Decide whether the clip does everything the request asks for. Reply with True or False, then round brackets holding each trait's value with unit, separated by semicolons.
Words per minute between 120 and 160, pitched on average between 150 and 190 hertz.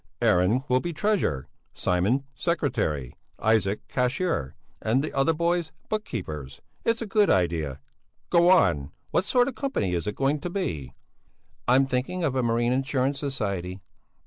False (155 wpm; 130 Hz)